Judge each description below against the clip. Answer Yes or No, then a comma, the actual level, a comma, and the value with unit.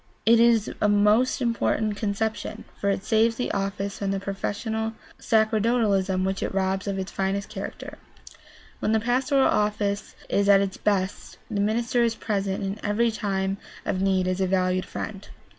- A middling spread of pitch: No, narrow, 2.3 semitones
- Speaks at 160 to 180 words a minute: Yes, average, 165 wpm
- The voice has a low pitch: No, high, 205 Hz